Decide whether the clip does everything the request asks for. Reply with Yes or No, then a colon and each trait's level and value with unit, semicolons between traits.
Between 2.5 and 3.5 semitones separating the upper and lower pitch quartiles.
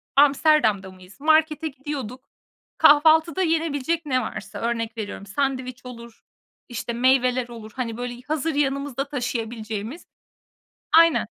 No: average, 4.2 semitones